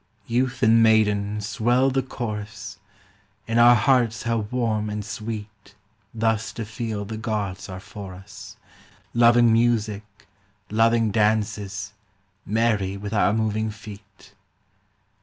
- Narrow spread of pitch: Yes, narrow, 1.9 semitones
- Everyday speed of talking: No, slow, 120 wpm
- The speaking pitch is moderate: No, low, 110 Hz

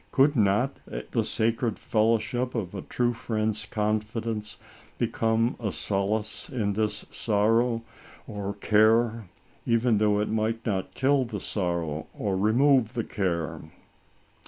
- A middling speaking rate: No, slow, 125 wpm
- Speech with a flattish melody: Yes, narrow, 2.2 semitones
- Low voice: Yes, low, 110 Hz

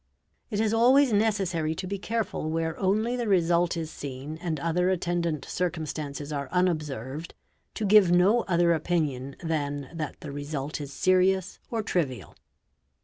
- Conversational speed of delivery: Yes, average, 145 wpm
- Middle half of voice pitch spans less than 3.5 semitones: No, average, 4.1 semitones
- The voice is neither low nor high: Yes, medium, 170 Hz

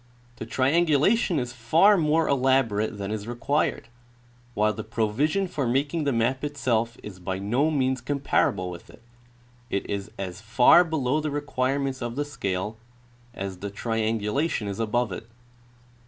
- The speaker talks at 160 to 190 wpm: No, average, 150 wpm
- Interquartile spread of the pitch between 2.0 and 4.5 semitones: No, average, 5.3 semitones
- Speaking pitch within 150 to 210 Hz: No, low, 120 Hz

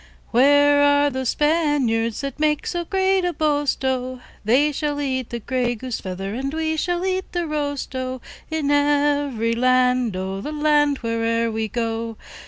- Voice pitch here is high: Yes, very high, 275 Hz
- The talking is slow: No, average, 165 wpm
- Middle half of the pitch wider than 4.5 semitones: No, average, 4.0 semitones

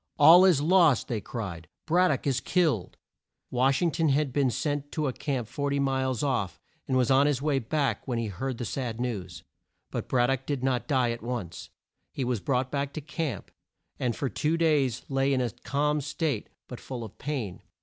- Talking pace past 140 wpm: Yes, average, 200 wpm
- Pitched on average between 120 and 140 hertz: Yes, low, 135 Hz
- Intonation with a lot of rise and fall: No, average, 3.2 semitones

